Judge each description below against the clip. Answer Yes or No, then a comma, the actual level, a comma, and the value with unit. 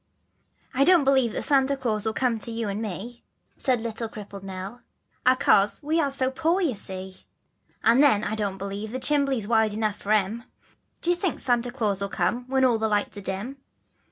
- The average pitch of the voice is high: Yes, high, 230 Hz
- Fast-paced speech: Yes, fast, 210 wpm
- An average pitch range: Yes, average, 4.4 semitones